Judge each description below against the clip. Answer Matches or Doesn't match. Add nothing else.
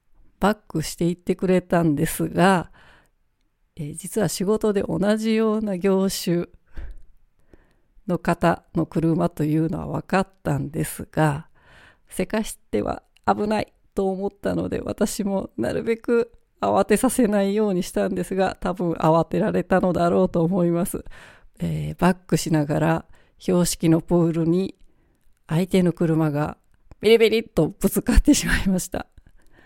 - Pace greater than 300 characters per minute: Doesn't match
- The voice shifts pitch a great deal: Doesn't match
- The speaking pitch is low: Doesn't match